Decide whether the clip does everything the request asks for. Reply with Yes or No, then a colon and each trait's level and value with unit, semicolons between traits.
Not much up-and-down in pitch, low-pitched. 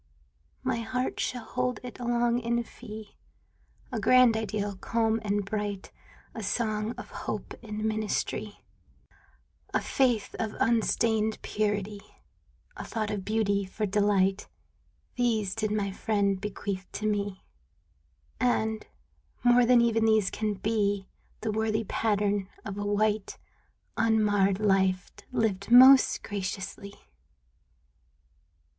No: narrow, 2.0 semitones; high, 215 Hz